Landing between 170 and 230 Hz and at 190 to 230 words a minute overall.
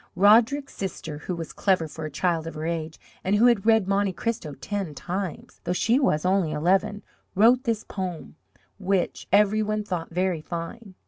No: high, 190 Hz; average, 180 wpm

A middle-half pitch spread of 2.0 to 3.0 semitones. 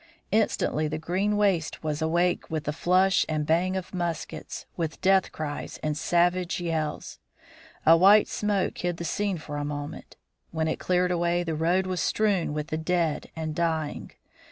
Yes: average, 2.7 semitones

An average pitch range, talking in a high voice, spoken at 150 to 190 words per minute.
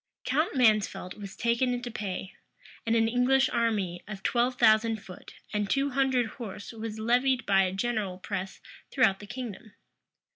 Yes: average, 3.6 semitones; high, 225 Hz; average, 155 wpm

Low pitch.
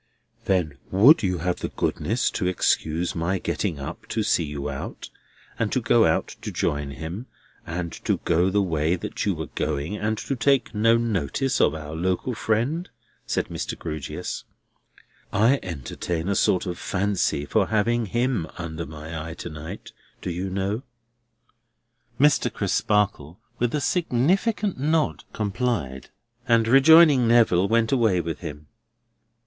Yes: very low, 95 Hz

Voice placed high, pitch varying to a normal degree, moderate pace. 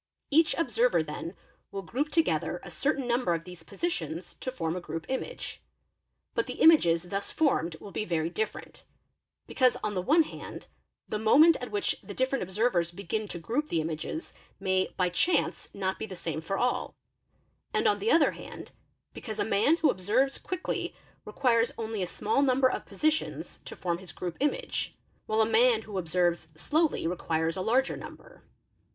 No: high, 215 Hz; wide, 7.6 semitones; average, 180 wpm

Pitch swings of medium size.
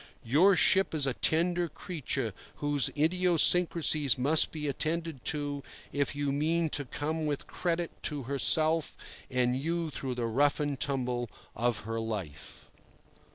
Yes: average, 4.0 semitones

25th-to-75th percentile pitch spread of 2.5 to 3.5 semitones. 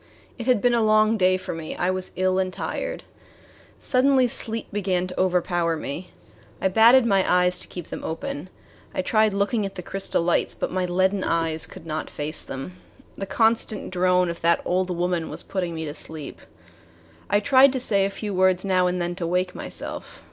Yes: average, 2.8 semitones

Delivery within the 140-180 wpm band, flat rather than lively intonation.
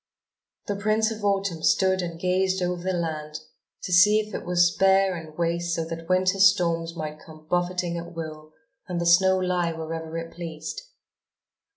Yes: average, 175 wpm; narrow, 2.3 semitones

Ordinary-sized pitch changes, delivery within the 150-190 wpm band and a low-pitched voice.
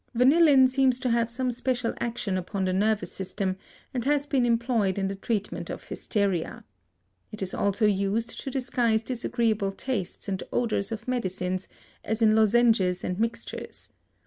No: average, 3.9 semitones; average, 155 wpm; high, 225 Hz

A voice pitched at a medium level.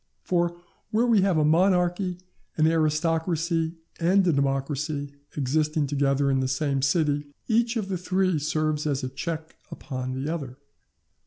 Yes: medium, 155 Hz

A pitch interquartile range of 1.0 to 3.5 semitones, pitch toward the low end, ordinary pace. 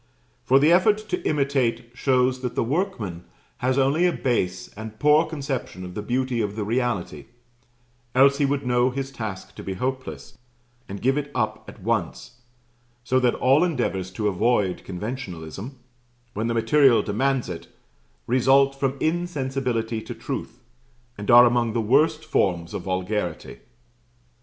No: average, 4.4 semitones; low, 125 Hz; average, 150 wpm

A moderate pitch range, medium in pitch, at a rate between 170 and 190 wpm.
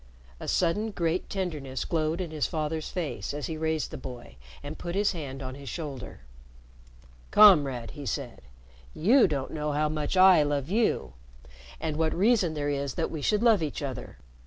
Yes: average, 3.9 semitones; medium, 155 Hz; average, 180 wpm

